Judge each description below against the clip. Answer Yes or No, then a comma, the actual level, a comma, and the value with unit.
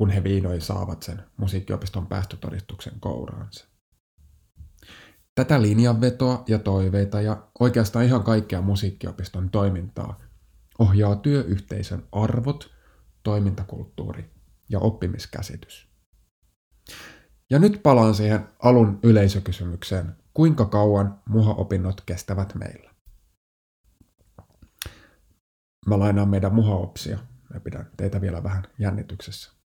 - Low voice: Yes, low, 100 Hz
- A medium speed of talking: No, slow, 90 wpm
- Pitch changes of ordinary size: Yes, average, 3.0 semitones